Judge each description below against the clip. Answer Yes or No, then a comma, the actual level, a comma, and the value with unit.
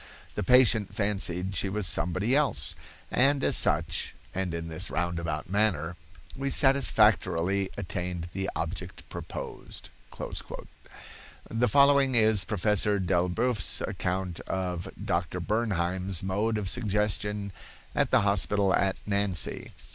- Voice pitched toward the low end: Yes, very low, 95 Hz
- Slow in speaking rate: Yes, slow, 115 wpm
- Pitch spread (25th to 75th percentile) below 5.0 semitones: Yes, average, 3.2 semitones